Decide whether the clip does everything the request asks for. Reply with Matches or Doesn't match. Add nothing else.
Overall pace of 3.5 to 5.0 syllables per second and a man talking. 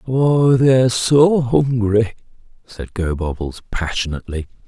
Matches